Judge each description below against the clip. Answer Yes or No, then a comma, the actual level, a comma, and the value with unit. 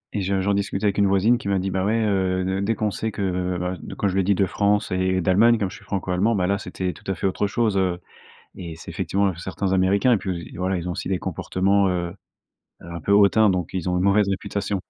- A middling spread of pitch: No, narrow, 1.6 semitones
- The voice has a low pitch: Yes, very low, 95 Hz